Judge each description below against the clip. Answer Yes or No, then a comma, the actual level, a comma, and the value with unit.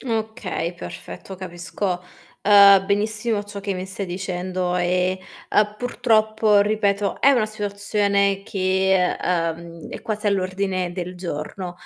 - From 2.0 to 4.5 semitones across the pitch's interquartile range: Yes, narrow, 2.4 semitones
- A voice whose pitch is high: Yes, high, 195 Hz